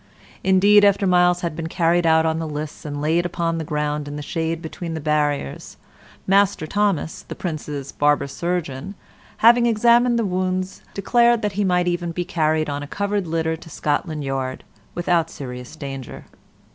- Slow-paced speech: No, average, 170 wpm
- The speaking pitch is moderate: Yes, medium, 165 Hz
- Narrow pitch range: No, average, 3.9 semitones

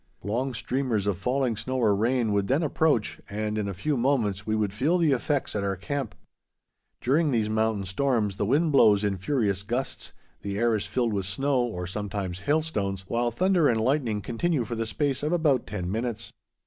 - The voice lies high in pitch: No, low, 115 Hz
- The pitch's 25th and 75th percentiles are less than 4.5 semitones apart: No, average, 5.0 semitones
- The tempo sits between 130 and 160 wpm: No, average, 195 wpm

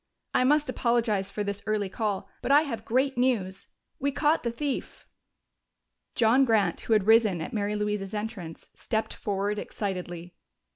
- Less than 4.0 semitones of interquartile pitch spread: Yes, average, 3.6 semitones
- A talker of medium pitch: No, high, 215 Hz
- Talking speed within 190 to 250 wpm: No, average, 155 wpm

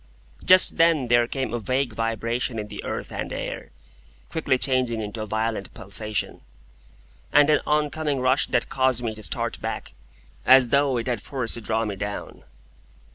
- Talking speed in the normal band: Yes, average, 170 wpm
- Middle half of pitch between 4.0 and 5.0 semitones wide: No, average, 3.3 semitones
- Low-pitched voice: Yes, low, 120 Hz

